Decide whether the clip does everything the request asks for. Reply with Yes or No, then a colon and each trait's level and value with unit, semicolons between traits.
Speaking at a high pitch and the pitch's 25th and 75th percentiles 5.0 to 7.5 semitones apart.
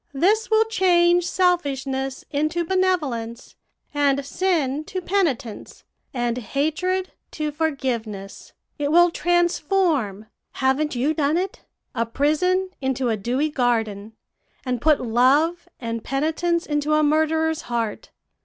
Yes: very high, 295 Hz; wide, 5.4 semitones